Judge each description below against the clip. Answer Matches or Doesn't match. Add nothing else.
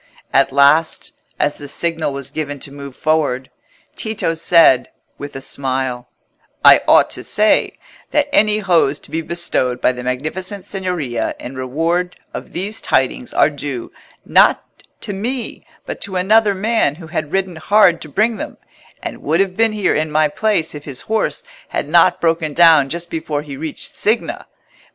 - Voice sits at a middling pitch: Matches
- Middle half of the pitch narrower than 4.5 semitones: Doesn't match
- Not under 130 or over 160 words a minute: Doesn't match